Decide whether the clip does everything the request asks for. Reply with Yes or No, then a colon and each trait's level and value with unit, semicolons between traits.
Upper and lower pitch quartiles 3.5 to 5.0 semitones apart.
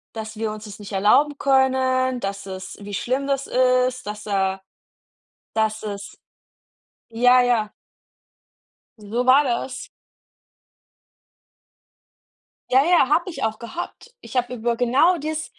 Yes: average, 3.8 semitones